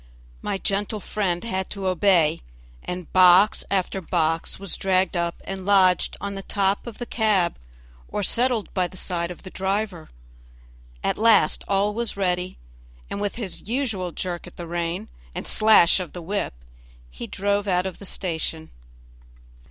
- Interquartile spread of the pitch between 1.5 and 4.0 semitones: Yes, narrow, 2.4 semitones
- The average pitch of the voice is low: No, high, 190 Hz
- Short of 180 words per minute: Yes, average, 160 wpm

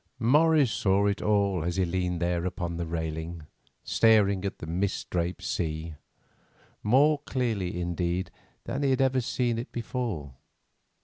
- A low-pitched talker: Yes, very low, 95 Hz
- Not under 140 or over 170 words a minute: Yes, average, 145 wpm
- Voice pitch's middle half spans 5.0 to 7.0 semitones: Yes, wide, 5.5 semitones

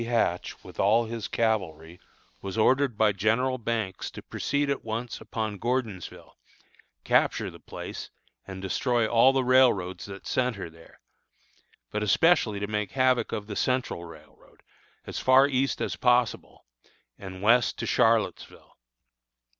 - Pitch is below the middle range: Yes, low, 110 Hz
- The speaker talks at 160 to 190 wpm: No, average, 140 wpm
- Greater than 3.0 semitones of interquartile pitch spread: Yes, average, 4.4 semitones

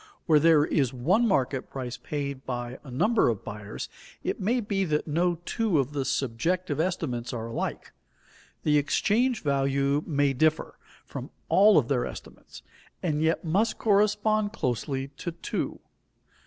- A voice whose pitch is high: No, medium, 150 Hz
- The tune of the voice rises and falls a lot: Yes, wide, 5.9 semitones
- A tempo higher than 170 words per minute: No, average, 150 wpm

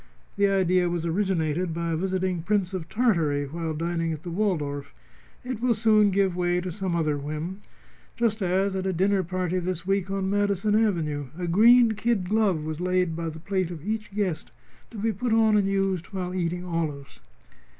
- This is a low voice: No, medium, 185 Hz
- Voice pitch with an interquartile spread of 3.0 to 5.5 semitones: Yes, average, 3.3 semitones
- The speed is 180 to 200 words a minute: Yes, average, 190 wpm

